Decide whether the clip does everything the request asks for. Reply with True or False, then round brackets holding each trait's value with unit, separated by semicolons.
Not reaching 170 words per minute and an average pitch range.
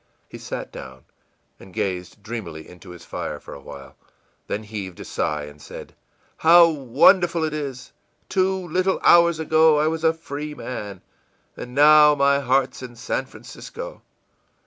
False (160 wpm; 8.1 semitones)